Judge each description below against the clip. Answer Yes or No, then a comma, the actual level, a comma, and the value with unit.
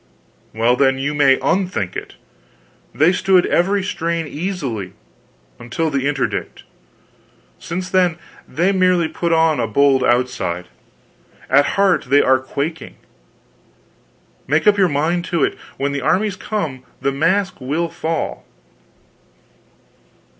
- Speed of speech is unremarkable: No, slow, 125 wpm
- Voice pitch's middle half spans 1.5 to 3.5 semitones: No, average, 5.1 semitones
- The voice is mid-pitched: Yes, medium, 160 Hz